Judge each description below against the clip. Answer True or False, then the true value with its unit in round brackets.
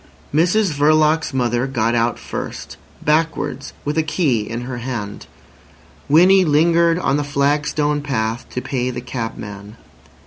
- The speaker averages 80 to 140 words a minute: True (135 wpm)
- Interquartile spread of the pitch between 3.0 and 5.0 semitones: True (4.5 semitones)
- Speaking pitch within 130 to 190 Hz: True (140 Hz)